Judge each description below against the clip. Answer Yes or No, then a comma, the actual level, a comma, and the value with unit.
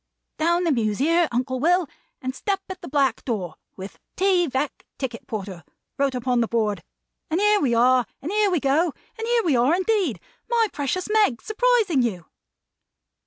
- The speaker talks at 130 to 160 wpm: No, average, 175 wpm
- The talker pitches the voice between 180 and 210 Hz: No, very high, 285 Hz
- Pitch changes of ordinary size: No, wide, 7.6 semitones